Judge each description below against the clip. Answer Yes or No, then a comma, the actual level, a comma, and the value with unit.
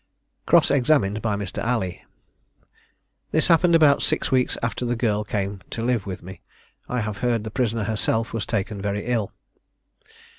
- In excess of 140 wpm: Yes, average, 160 wpm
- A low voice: Yes, low, 115 Hz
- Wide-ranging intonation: No, average, 3.3 semitones